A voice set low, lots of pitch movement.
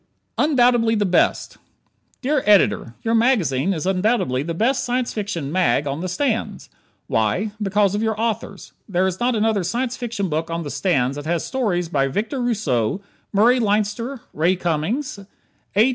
No: high, 205 Hz; wide, 5.7 semitones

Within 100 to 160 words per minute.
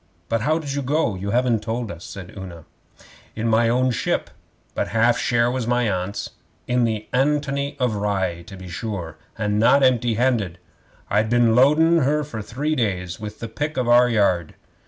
No: average, 185 wpm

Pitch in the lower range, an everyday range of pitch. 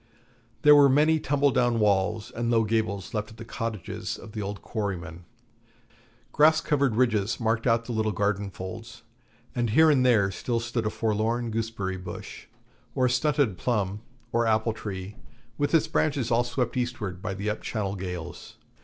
Yes: low, 115 Hz; average, 3.3 semitones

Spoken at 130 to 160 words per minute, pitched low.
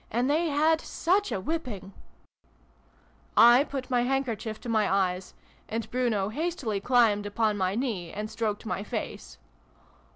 No: average, 150 wpm; high, 230 Hz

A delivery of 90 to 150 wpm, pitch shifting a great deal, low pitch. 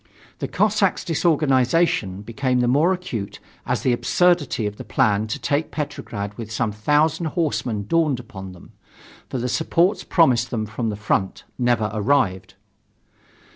Yes: average, 145 wpm; wide, 6.7 semitones; low, 125 Hz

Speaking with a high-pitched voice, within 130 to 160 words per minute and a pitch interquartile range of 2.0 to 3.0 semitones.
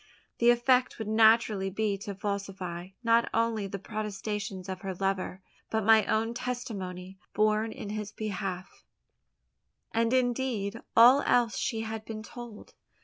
Yes: high, 215 Hz; average, 140 wpm; average, 2.7 semitones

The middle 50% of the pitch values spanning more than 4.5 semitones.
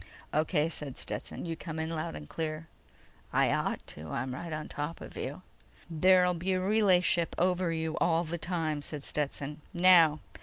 No: narrow, 2.6 semitones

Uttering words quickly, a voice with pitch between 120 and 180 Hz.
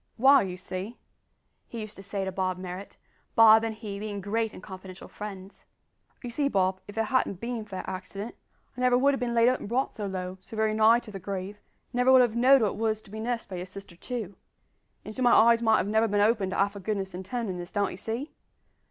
No: fast, 250 wpm; high, 215 Hz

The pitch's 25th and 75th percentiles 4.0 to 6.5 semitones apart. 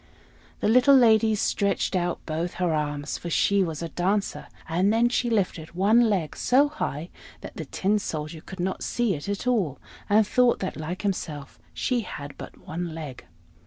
Yes: average, 5.3 semitones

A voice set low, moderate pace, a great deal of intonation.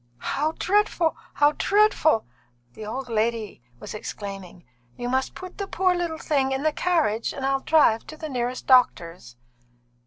No: very high, 270 Hz; average, 155 wpm; wide, 6.1 semitones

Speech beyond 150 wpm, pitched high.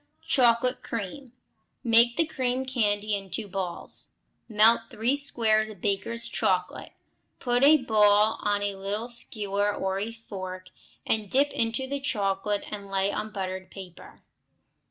No: slow, 135 wpm; high, 215 Hz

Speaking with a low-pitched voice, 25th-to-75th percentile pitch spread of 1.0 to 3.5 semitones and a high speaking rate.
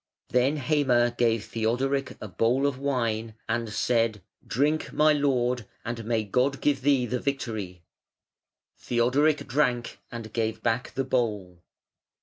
No: low, 120 Hz; average, 3.2 semitones; slow, 135 wpm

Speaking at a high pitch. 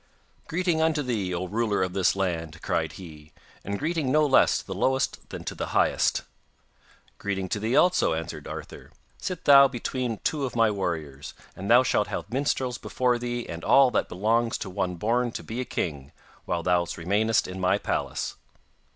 No: low, 110 Hz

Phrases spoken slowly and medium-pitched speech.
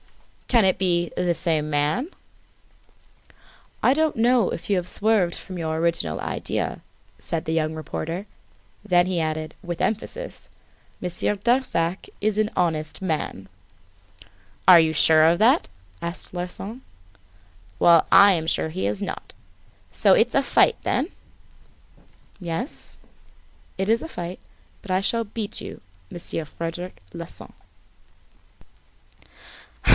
Yes: slow, 130 wpm; medium, 175 Hz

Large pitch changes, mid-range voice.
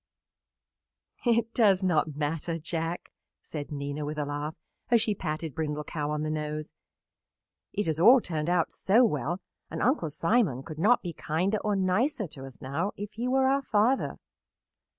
Yes: wide, 5.8 semitones; medium, 165 Hz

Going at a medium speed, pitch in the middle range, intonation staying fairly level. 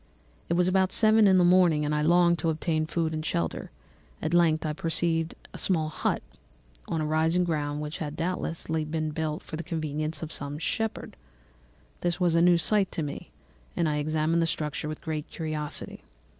Yes: average, 190 wpm; medium, 160 Hz; narrow, 2.1 semitones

